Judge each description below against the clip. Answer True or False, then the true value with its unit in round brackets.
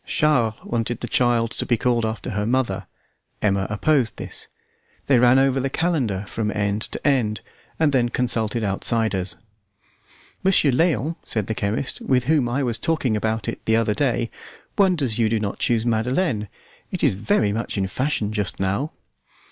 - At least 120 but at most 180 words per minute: True (170 wpm)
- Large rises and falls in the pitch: False (3.8 semitones)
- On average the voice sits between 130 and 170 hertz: False (115 Hz)